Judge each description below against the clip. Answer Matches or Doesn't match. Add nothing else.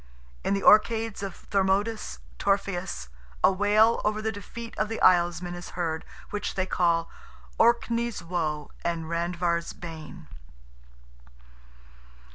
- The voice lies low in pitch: Doesn't match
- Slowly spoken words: Matches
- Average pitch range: Matches